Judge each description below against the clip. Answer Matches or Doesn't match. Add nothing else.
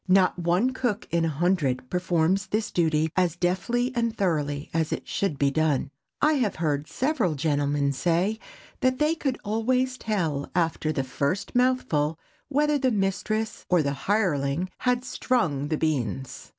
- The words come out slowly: Doesn't match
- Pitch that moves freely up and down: Matches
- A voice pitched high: Doesn't match